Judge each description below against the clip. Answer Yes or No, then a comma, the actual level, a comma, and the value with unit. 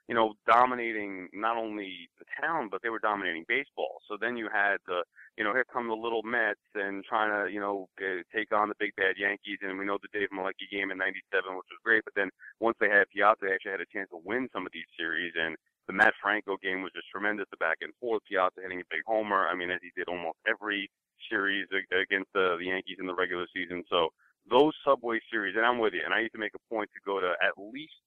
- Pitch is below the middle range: Yes, low, 100 Hz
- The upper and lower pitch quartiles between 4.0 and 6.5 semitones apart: No, average, 3.1 semitones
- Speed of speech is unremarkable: No, fast, 250 wpm